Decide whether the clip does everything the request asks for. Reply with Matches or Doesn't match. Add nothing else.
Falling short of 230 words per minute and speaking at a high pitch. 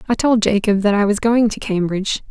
Doesn't match